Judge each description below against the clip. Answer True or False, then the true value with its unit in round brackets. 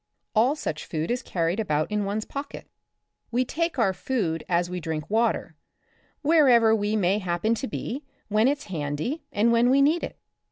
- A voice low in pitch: False (220 Hz)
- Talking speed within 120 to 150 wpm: False (175 wpm)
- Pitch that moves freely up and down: True (6.4 semitones)